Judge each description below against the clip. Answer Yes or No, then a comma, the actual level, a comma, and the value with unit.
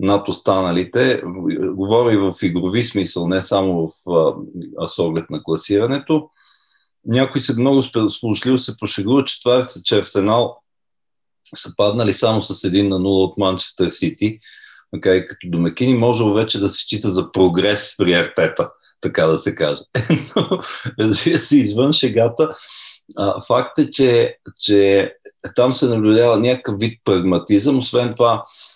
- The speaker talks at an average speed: Yes, average, 140 wpm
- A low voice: Yes, low, 115 Hz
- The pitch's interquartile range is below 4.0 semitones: No, average, 4.7 semitones